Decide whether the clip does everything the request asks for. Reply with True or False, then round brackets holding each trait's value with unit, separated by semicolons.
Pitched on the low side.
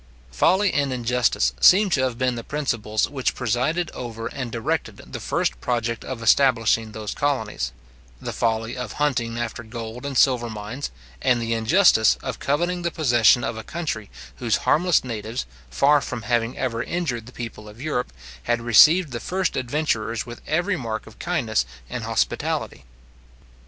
True (120 Hz)